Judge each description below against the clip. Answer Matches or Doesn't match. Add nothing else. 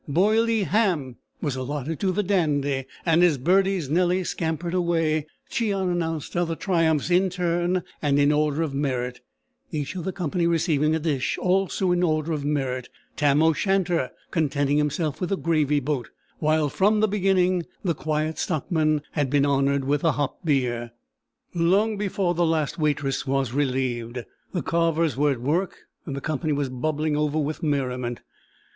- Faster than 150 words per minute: Matches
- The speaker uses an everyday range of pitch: Matches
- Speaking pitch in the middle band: Matches